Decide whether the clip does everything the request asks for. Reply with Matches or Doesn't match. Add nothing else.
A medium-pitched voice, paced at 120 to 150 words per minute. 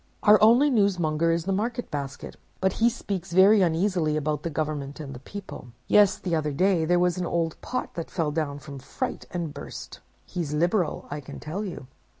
Doesn't match